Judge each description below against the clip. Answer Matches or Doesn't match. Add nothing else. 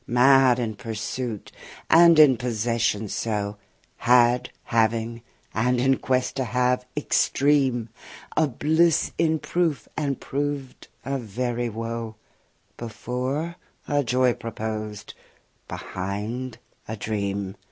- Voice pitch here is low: Matches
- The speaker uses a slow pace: Matches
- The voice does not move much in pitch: Doesn't match